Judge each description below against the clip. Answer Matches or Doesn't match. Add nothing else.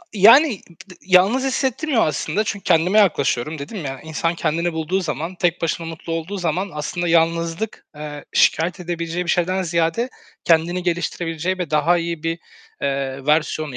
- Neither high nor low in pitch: Matches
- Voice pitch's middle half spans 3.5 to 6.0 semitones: Doesn't match